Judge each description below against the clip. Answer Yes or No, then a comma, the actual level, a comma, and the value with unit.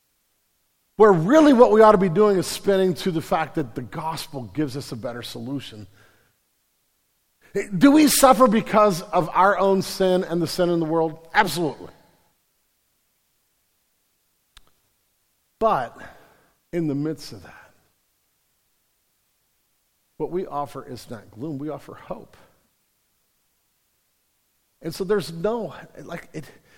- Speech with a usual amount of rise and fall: No, wide, 7.3 semitones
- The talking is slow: Yes, slow, 130 wpm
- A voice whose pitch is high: No, medium, 165 Hz